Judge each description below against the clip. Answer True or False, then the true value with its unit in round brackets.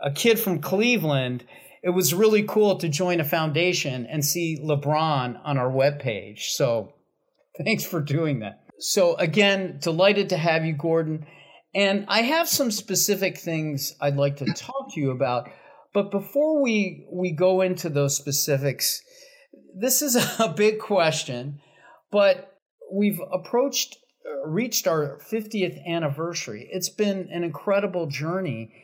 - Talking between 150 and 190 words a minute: False (140 wpm)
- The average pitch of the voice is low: False (180 Hz)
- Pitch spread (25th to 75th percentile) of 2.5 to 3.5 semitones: False (5.4 semitones)